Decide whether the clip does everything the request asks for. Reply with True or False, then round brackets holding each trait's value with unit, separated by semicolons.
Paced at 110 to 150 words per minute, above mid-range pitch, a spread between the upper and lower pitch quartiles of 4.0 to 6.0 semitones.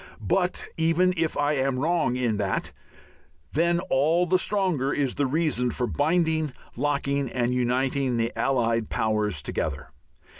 False (140 wpm; 140 Hz; 4.8 semitones)